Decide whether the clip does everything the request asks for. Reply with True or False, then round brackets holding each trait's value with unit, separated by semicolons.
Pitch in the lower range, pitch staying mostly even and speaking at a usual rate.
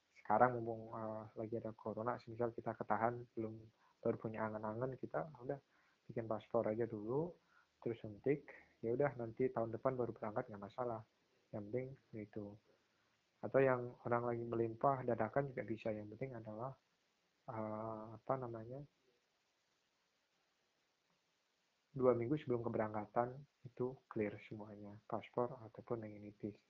True (115 Hz; 2.1 semitones; 130 wpm)